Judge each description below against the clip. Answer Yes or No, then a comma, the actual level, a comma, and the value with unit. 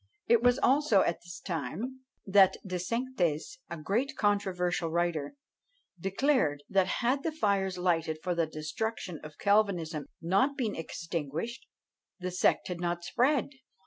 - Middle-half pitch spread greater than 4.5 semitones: Yes, wide, 5.6 semitones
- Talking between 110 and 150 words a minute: Yes, average, 140 wpm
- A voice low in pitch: No, medium, 185 Hz